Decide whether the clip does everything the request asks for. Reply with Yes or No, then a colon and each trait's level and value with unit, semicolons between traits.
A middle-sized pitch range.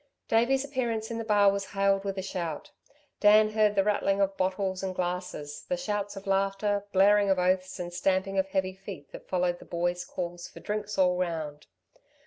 No: narrow, 2.2 semitones